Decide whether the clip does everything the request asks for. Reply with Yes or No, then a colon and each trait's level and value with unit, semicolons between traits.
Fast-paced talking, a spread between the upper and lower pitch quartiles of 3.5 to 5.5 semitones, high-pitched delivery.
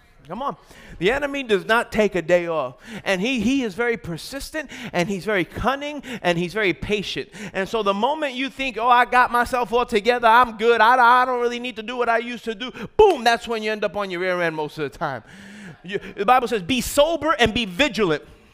Yes: fast, 235 wpm; average, 4.0 semitones; high, 230 Hz